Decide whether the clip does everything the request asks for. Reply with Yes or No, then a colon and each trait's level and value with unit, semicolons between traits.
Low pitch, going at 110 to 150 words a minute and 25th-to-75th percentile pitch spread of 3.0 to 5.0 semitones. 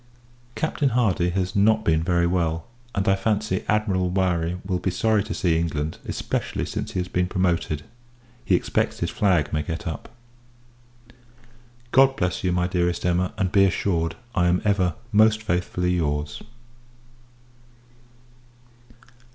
No: very low, 90 Hz; average, 145 wpm; narrow, 2.6 semitones